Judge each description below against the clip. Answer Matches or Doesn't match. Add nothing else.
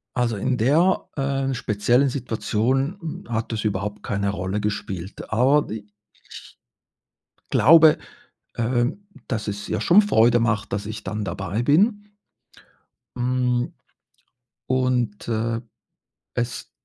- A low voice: Matches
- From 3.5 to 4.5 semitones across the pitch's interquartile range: Matches